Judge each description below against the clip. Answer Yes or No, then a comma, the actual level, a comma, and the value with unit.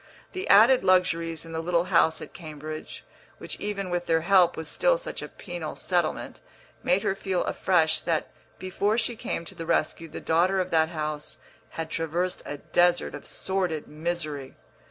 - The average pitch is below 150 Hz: No, medium, 170 Hz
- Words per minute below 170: No, average, 175 wpm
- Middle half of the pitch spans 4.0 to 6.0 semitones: No, average, 2.7 semitones